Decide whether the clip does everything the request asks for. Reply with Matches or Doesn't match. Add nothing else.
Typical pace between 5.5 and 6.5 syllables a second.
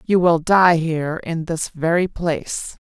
Doesn't match